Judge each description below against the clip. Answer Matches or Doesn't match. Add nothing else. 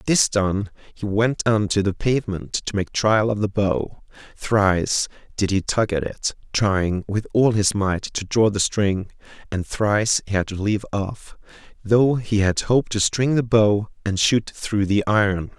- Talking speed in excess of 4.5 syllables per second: Doesn't match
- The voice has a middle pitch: Doesn't match